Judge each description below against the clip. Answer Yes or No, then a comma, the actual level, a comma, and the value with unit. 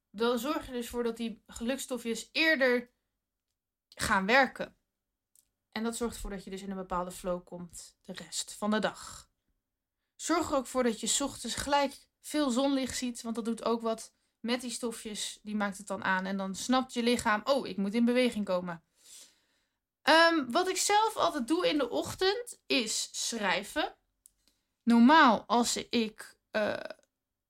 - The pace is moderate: Yes, average, 170 wpm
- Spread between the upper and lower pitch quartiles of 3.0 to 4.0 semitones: No, average, 5.0 semitones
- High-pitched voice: Yes, high, 235 Hz